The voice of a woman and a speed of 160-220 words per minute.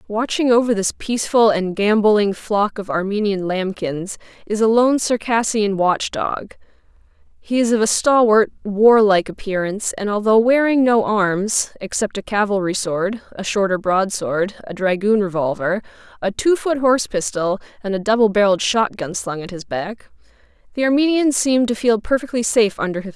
Yes: female; average, 165 wpm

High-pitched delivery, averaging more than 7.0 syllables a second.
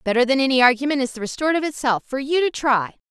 Yes: very high, 265 Hz; 7.3 syllables/s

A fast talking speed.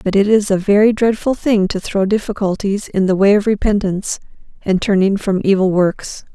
No: average, 190 wpm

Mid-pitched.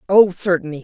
Yes: medium, 175 Hz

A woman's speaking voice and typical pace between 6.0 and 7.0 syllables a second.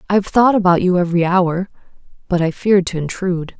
Yes: female; 6.4 syllables/s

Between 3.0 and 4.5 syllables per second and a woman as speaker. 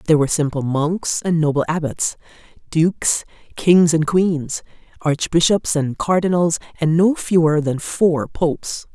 Yes: 4.3 syllables/s; female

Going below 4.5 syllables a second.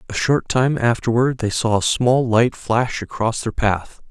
Yes: 4.1 syllables/s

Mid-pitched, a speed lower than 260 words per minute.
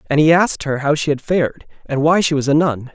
No: medium, 150 Hz; fast, 285 wpm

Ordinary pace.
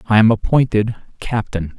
Yes: average, 170 wpm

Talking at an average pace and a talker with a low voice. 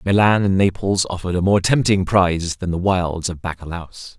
Yes: average, 185 wpm; very low, 90 Hz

